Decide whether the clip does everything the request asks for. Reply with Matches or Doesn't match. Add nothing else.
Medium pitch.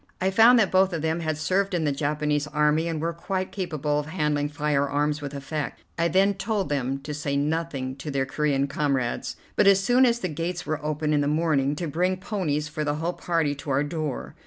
Matches